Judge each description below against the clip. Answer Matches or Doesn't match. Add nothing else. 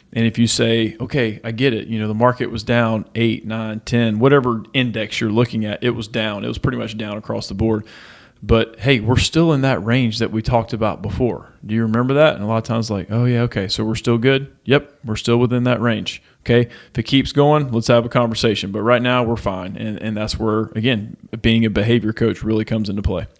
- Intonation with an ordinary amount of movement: Doesn't match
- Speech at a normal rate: Doesn't match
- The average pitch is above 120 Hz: Doesn't match